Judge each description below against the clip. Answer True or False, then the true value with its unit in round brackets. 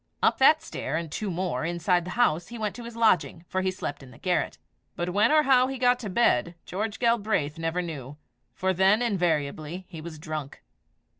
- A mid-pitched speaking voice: True (180 Hz)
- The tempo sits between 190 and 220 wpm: True (205 wpm)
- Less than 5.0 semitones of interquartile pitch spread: False (5.6 semitones)